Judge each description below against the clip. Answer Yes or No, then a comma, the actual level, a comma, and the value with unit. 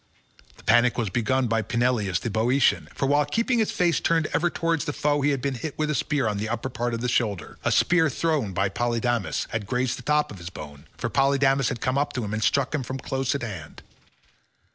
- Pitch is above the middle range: No, low, 125 Hz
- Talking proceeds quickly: Yes, fast, 235 wpm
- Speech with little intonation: No, average, 4.3 semitones